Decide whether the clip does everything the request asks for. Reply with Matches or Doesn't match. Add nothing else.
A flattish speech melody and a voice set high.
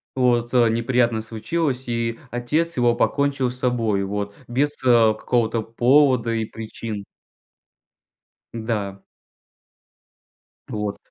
Doesn't match